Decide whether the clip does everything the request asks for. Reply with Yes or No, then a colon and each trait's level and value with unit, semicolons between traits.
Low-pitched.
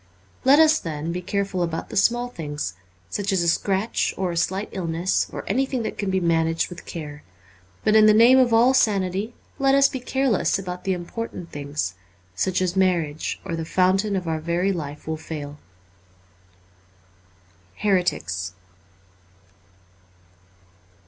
No: medium, 180 Hz